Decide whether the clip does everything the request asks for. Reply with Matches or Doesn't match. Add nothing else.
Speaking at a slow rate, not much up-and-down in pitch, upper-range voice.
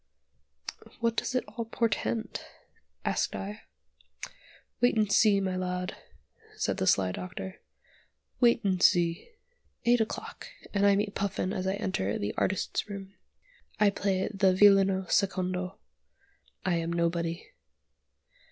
Matches